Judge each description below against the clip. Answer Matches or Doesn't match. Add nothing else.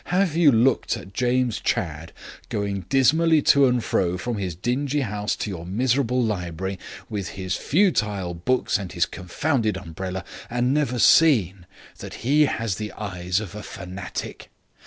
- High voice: Doesn't match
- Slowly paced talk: Doesn't match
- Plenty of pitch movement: Matches